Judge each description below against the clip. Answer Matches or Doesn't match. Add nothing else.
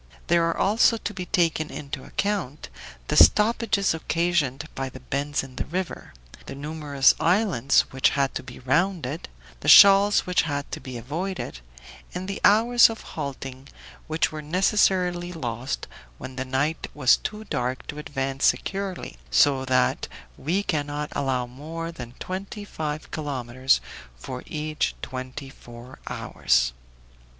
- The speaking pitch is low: Doesn't match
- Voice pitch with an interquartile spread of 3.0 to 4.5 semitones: Doesn't match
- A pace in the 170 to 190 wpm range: Doesn't match